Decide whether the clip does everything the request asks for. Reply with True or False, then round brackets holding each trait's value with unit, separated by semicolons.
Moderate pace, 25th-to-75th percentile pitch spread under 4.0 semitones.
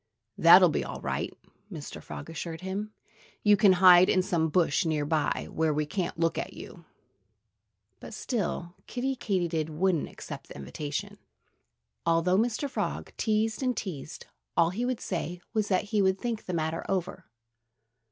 False (160 wpm; 4.3 semitones)